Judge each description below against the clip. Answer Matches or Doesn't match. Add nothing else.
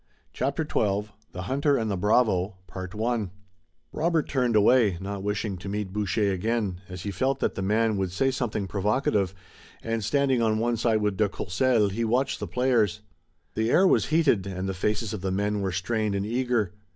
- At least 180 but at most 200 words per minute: Matches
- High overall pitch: Doesn't match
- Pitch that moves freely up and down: Doesn't match